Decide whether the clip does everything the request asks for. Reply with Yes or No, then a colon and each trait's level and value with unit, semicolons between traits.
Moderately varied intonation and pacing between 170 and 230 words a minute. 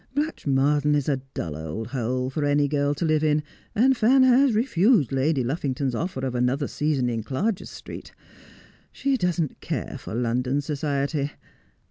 No: average, 4.3 semitones; average, 160 wpm